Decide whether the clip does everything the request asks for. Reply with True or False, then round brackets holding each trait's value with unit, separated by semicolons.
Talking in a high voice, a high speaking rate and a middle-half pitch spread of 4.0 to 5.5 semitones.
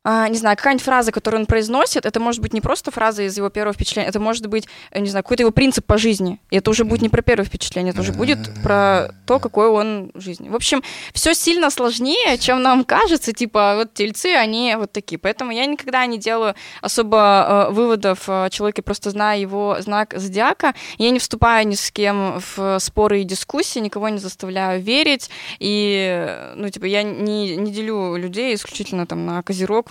False (210 Hz; 195 wpm; 2.9 semitones)